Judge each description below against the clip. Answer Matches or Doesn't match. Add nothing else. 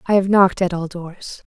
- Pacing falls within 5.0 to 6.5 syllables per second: Matches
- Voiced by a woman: Matches